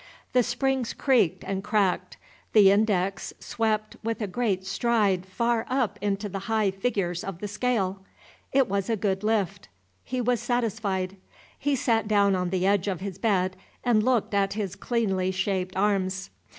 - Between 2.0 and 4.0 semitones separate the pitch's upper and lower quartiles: Yes, average, 3.2 semitones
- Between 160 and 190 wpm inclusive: Yes, average, 165 wpm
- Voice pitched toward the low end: No, high, 205 Hz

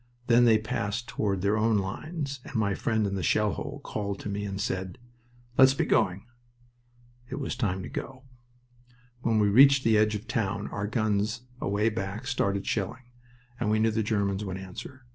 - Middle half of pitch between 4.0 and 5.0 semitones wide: No, average, 3.1 semitones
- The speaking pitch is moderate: No, low, 105 Hz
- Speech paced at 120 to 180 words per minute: No, average, 190 wpm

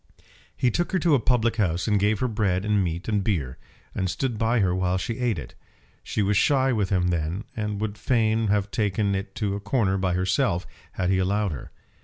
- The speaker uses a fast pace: Yes, fast, 220 wpm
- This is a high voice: No, low, 100 Hz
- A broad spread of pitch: No, average, 3.3 semitones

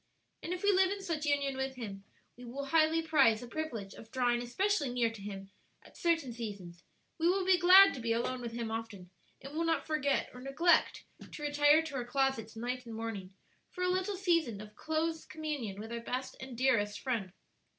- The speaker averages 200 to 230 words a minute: Yes, fast, 205 wpm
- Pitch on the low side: No, very high, 265 Hz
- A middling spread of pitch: No, wide, 5.9 semitones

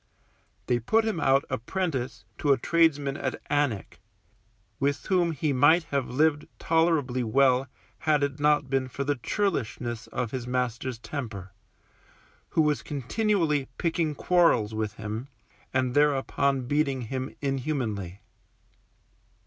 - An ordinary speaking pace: No, slow, 125 wpm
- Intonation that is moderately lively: Yes, average, 3.6 semitones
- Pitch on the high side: No, medium, 140 Hz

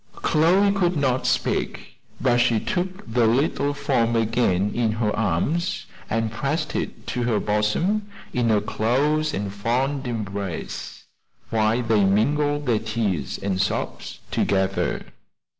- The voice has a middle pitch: No, low, 115 Hz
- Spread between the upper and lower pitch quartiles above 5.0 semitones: Yes, wide, 5.4 semitones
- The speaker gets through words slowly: Yes, slow, 130 wpm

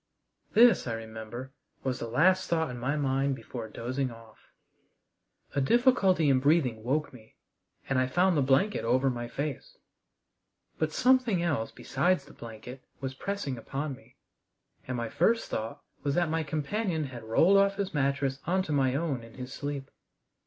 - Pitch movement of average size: Yes, average, 5.0 semitones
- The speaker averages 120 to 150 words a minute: No, average, 165 wpm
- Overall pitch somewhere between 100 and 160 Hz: Yes, medium, 140 Hz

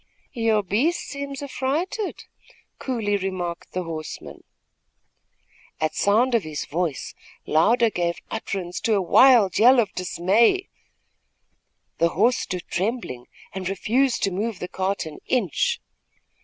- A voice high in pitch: Yes, high, 200 Hz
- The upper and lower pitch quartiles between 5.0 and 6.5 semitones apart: Yes, wide, 5.6 semitones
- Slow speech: Yes, slow, 125 wpm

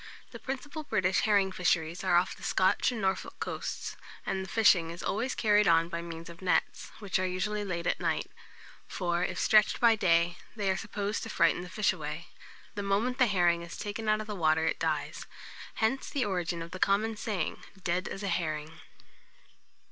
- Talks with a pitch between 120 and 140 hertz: No, high, 190 Hz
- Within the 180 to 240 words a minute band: Yes, average, 195 wpm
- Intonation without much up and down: No, average, 3.7 semitones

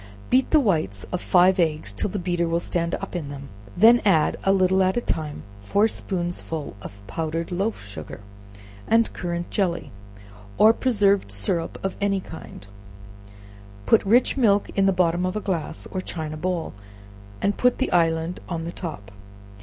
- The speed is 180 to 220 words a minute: No, average, 170 wpm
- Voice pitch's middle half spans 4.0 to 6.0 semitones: No, average, 3.5 semitones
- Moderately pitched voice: Yes, medium, 175 Hz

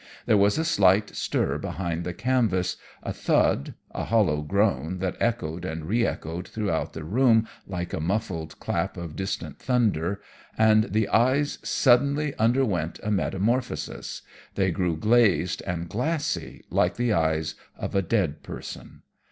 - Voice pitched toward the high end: No, low, 100 Hz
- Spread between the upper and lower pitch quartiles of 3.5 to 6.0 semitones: Yes, wide, 5.4 semitones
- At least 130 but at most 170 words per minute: Yes, average, 145 wpm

